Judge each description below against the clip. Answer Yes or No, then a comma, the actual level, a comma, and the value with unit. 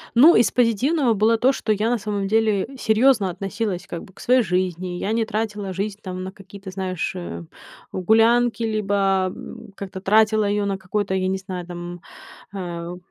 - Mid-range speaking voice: No, high, 200 Hz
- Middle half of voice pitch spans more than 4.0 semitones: No, average, 3.0 semitones